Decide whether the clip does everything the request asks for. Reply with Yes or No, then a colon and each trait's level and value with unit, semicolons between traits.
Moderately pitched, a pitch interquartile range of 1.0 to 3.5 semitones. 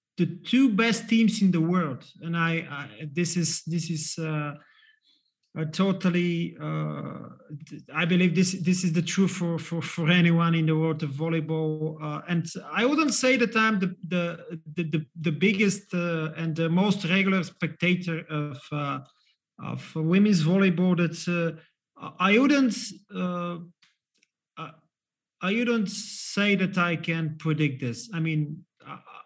Yes: medium, 170 Hz; average, 2.9 semitones